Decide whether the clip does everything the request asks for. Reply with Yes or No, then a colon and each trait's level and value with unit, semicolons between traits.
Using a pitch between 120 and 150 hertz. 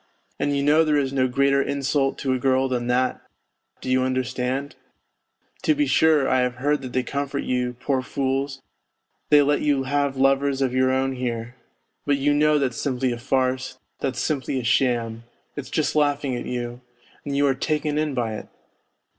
Yes: low, 135 Hz